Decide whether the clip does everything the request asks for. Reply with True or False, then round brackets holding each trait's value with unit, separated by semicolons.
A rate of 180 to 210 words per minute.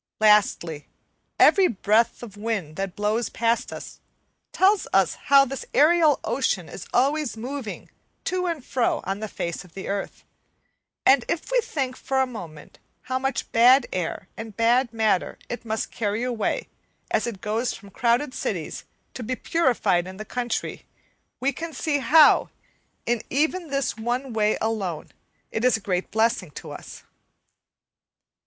False (155 wpm)